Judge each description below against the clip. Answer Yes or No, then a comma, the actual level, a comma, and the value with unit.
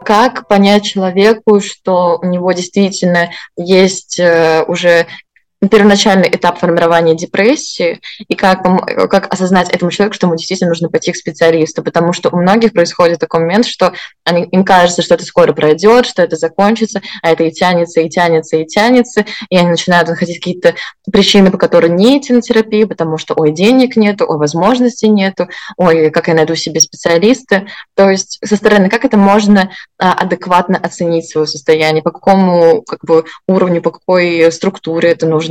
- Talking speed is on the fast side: Yes, fast, 165 wpm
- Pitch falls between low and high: Yes, medium, 180 Hz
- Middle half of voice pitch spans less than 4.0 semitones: Yes, average, 3.3 semitones